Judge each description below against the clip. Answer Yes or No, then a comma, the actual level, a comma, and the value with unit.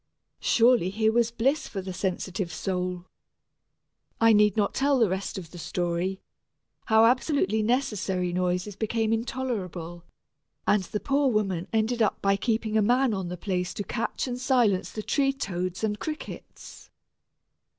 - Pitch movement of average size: Yes, average, 4.4 semitones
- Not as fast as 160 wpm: Yes, average, 150 wpm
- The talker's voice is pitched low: No, high, 210 Hz